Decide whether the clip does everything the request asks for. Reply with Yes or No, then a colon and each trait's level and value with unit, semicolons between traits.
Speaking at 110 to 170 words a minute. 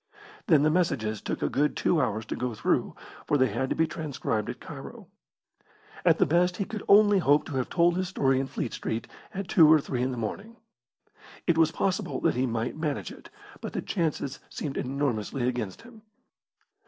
No: average, 200 wpm